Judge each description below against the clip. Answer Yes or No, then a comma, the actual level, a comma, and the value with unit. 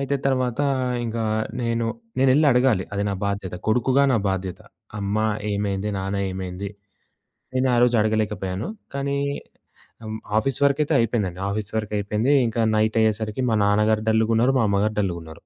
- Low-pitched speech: Yes, low, 110 Hz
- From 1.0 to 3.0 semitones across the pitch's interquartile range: No, average, 3.5 semitones